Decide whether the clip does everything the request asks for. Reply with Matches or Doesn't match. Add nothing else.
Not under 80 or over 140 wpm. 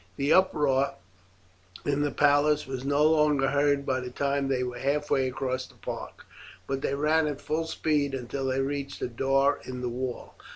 Doesn't match